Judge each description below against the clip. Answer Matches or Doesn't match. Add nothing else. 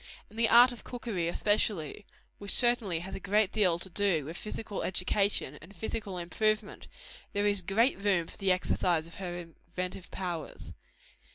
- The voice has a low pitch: Doesn't match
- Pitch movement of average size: Matches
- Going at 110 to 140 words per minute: Doesn't match